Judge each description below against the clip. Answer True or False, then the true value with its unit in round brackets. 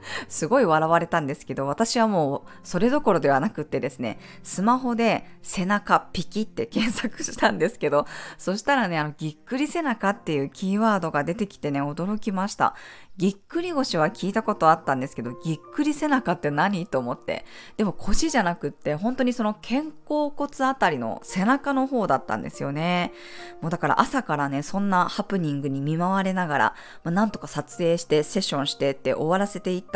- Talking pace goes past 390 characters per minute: True (400 characters per minute)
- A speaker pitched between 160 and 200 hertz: True (185 Hz)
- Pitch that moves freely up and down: True (6.7 semitones)